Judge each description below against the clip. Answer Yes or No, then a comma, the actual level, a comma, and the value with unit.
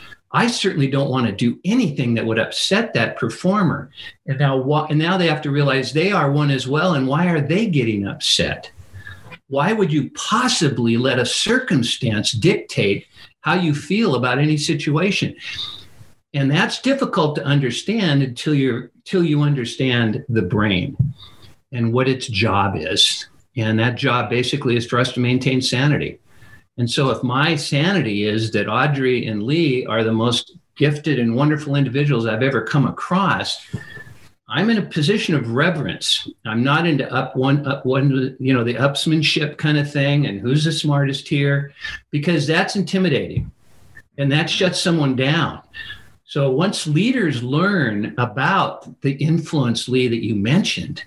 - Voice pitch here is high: No, medium, 140 Hz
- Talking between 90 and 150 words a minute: No, average, 160 wpm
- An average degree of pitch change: Yes, average, 4.4 semitones